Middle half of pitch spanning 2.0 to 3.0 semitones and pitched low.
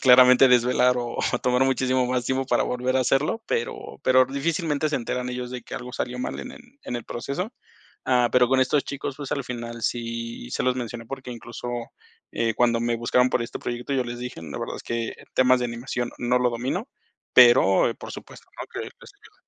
No: narrow, 1.6 semitones; low, 125 Hz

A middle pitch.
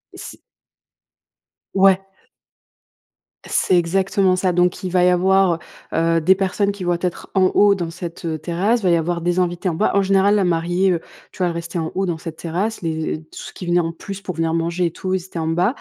Yes: medium, 180 Hz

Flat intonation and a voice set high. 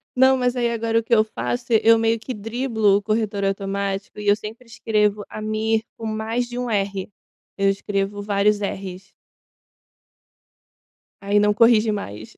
Yes: narrow, 2.2 semitones; high, 215 Hz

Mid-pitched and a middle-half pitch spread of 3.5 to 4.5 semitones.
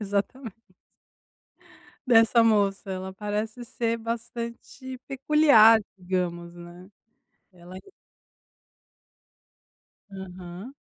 No: high, 210 Hz; average, 4.0 semitones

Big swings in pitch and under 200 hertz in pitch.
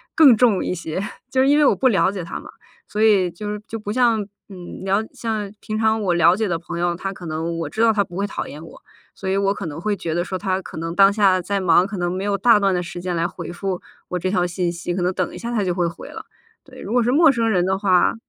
No: average, 3.5 semitones; high, 190 Hz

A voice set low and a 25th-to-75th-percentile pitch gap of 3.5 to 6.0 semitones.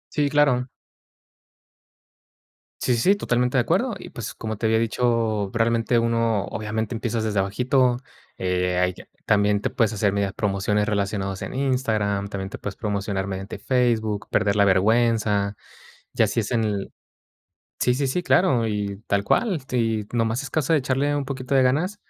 Yes: low, 110 Hz; average, 3.8 semitones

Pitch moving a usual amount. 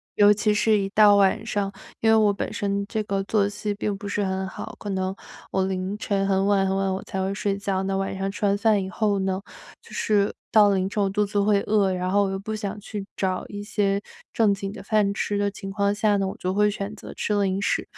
No: narrow, 1.2 semitones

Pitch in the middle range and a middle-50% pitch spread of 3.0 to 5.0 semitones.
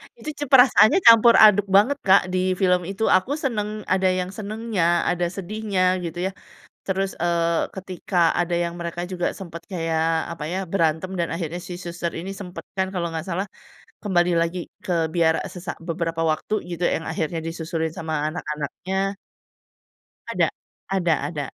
No: medium, 180 Hz; narrow, 2.5 semitones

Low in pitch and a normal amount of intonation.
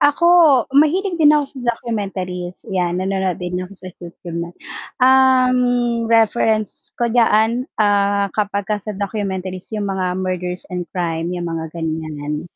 No: high, 195 Hz; average, 4.2 semitones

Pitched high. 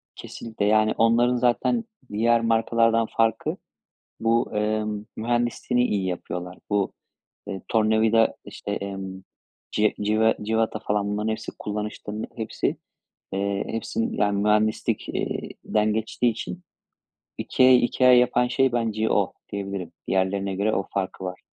No: low, 110 Hz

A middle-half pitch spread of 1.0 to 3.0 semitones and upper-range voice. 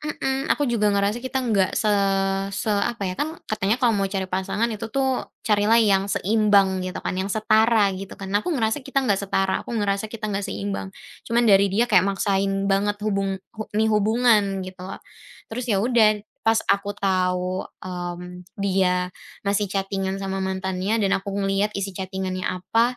Yes: narrow, 2.4 semitones; high, 200 Hz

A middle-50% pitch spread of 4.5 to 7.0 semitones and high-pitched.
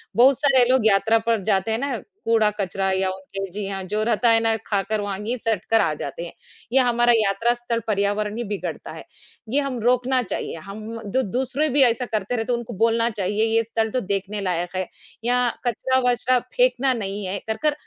No: average, 3.6 semitones; high, 225 Hz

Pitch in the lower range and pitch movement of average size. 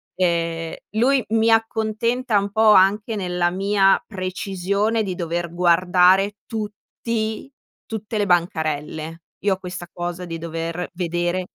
No: medium, 185 Hz; average, 3.7 semitones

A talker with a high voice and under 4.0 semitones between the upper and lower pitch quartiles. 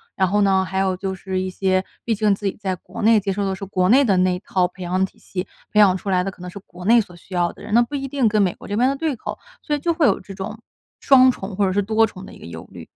Yes: high, 195 Hz; average, 2.8 semitones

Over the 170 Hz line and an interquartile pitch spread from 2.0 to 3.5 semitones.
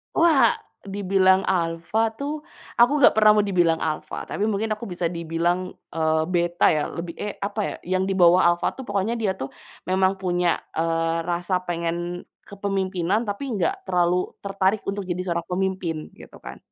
Yes: medium, 185 Hz; average, 2.8 semitones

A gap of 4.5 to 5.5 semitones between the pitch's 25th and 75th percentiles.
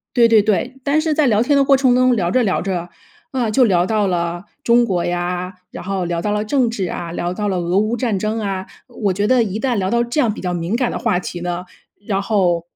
Yes: average, 5.0 semitones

